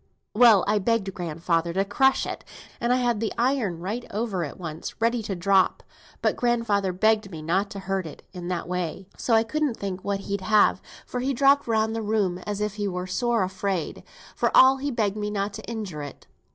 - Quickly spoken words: Yes, fast, 210 wpm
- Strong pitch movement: No, average, 3.8 semitones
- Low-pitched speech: No, high, 205 Hz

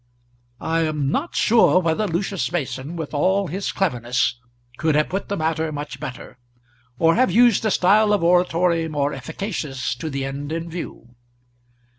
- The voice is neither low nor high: Yes, medium, 165 Hz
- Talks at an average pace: Yes, average, 160 wpm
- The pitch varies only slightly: No, average, 4.6 semitones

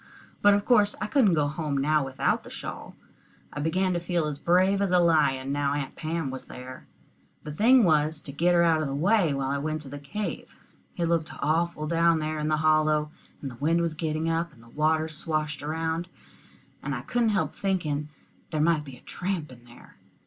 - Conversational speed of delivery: No, fast, 210 wpm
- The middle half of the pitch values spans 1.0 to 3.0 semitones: Yes, average, 2.7 semitones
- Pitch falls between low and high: Yes, medium, 155 Hz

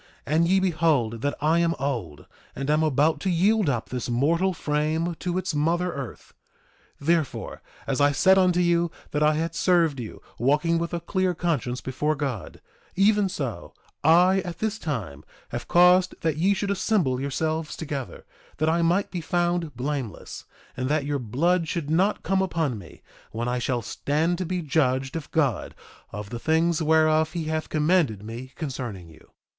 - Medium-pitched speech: Yes, medium, 155 Hz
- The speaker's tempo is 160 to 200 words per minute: Yes, average, 175 wpm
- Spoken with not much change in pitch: No, average, 4.4 semitones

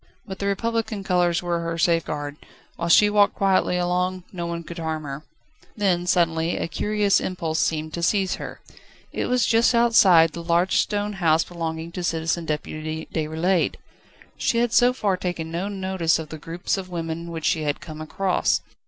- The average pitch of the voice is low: No, medium, 175 Hz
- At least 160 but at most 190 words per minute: Yes, average, 180 wpm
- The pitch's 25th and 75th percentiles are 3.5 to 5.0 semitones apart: No, average, 3.0 semitones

